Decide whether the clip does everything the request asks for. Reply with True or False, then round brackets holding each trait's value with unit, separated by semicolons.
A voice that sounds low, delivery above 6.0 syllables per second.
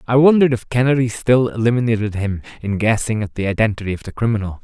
True (115 Hz; 6.7 syllables/s)